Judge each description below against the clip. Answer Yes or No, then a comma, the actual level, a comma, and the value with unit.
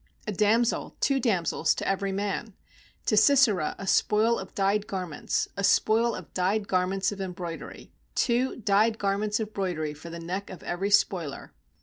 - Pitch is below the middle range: No, high, 200 Hz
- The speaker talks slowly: No, average, 165 wpm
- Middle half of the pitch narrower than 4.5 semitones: Yes, average, 2.9 semitones